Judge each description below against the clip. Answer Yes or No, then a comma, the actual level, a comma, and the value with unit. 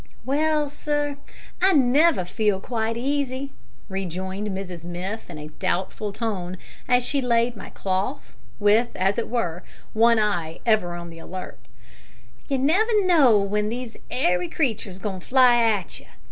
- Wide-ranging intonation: Yes, wide, 5.8 semitones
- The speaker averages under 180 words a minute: Yes, average, 155 wpm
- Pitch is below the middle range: No, high, 220 Hz